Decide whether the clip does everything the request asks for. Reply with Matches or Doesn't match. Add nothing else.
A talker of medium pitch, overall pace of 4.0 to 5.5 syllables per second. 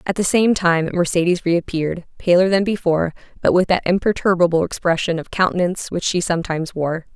Doesn't match